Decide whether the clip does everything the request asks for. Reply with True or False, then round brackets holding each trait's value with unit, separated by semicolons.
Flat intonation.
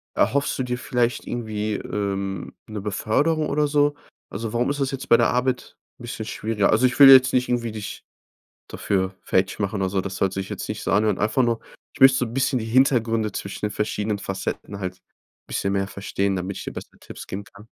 False (4.2 semitones)